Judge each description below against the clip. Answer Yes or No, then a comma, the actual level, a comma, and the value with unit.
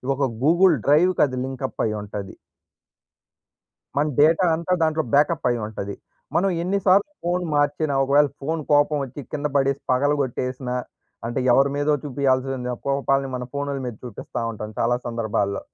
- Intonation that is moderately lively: Yes, average, 3.4 semitones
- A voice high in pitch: No, medium, 140 Hz